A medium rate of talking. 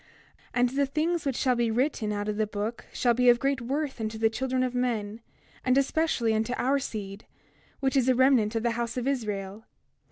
No: fast, 215 wpm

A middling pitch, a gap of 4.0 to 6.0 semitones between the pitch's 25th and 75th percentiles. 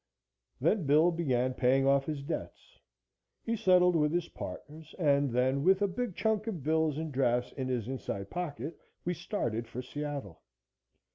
Yes: medium, 150 Hz; average, 5.2 semitones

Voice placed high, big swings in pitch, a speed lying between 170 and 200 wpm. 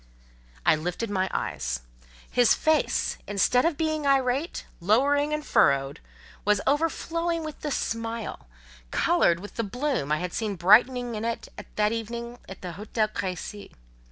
No: high, 230 Hz; wide, 6.7 semitones; average, 140 wpm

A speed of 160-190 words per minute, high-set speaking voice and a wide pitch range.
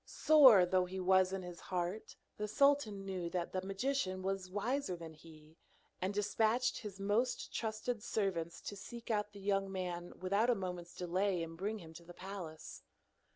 No: average, 175 wpm; high, 195 Hz; average, 2.9 semitones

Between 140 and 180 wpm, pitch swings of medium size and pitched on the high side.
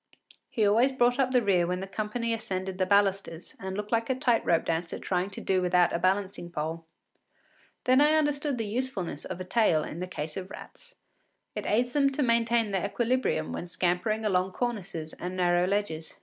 No: average, 195 wpm; average, 4.9 semitones; high, 195 Hz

